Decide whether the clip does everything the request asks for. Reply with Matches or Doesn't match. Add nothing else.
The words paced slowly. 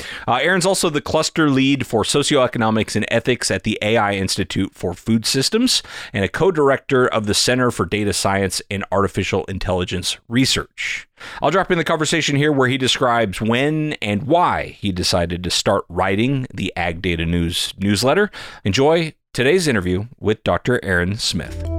Doesn't match